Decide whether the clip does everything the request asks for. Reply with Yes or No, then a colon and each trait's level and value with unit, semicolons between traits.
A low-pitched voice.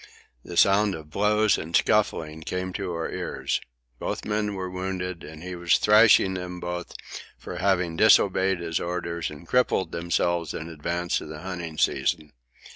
Yes: very low, 90 Hz